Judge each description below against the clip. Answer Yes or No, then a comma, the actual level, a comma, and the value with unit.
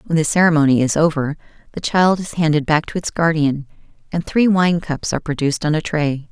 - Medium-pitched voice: Yes, medium, 155 Hz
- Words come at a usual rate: No, fast, 210 wpm